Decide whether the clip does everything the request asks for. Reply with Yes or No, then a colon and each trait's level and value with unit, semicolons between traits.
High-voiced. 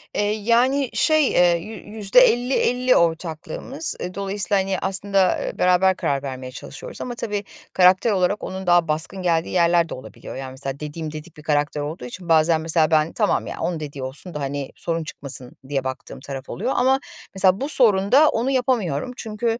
No: medium, 180 Hz